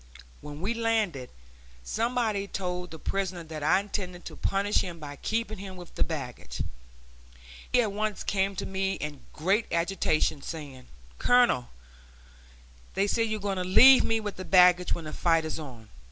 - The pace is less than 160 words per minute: No, average, 170 wpm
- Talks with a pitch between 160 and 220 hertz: Yes, medium, 185 Hz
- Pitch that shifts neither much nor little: Yes, average, 4.5 semitones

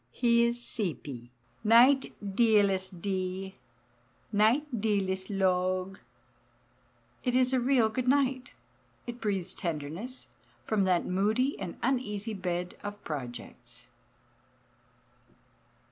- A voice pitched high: Yes, high, 205 Hz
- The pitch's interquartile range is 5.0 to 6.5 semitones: No, average, 4.4 semitones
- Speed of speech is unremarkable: No, slow, 100 wpm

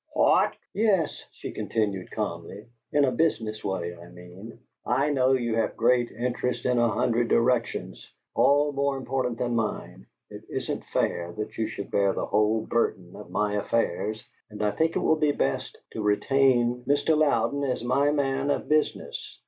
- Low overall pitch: Yes, low, 120 Hz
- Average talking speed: Yes, average, 170 wpm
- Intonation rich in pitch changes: No, average, 4.6 semitones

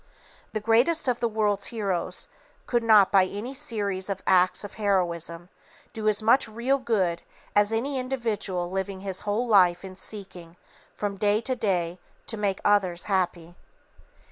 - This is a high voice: Yes, high, 205 Hz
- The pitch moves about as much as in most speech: Yes, average, 3.2 semitones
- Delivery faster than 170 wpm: No, average, 155 wpm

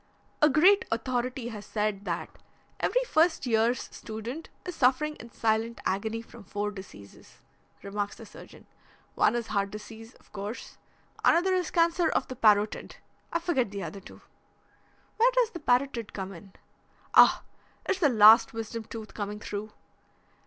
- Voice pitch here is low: No, high, 225 Hz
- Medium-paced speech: Yes, average, 150 wpm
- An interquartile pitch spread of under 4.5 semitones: No, average, 5.3 semitones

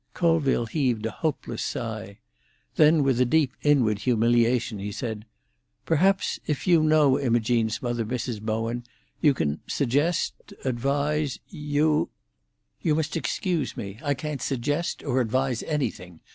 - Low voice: Yes, low, 130 Hz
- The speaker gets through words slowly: Yes, slow, 125 wpm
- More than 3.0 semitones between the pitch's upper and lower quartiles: Yes, average, 4.5 semitones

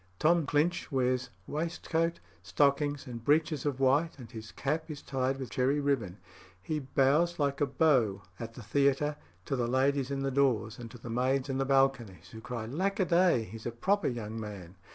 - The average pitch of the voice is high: No, low, 135 Hz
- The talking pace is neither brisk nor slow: Yes, average, 185 wpm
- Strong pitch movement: No, average, 3.9 semitones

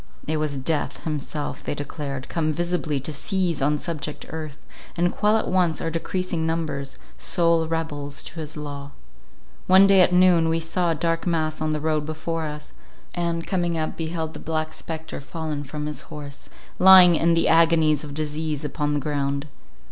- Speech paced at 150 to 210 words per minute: Yes, average, 180 wpm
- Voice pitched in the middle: Yes, medium, 160 Hz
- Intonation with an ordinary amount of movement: No, narrow, 2.1 semitones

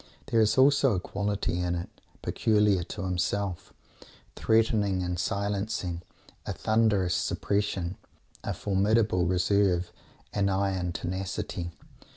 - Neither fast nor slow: No, slow, 110 wpm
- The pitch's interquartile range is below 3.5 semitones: Yes, narrow, 2.6 semitones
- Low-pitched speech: Yes, low, 100 Hz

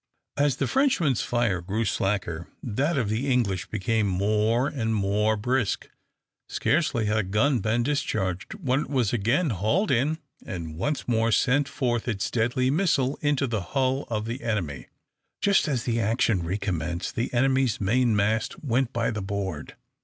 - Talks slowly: No, average, 165 wpm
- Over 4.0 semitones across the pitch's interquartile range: Yes, average, 4.6 semitones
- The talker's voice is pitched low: Yes, low, 115 Hz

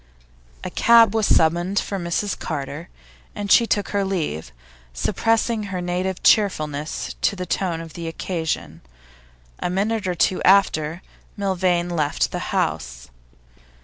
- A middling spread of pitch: Yes, average, 3.7 semitones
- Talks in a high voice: No, medium, 180 Hz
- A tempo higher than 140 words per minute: No, slow, 135 wpm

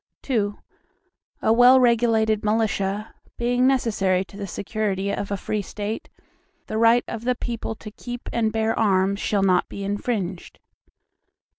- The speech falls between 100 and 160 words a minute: Yes, average, 145 wpm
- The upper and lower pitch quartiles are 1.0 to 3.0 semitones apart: Yes, average, 2.7 semitones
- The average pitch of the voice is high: Yes, high, 215 Hz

